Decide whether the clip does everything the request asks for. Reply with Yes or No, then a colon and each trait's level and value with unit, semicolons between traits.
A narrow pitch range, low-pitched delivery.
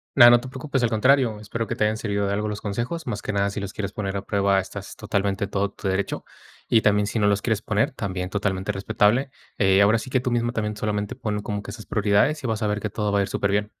Yes: narrow, 2.0 semitones; low, 105 Hz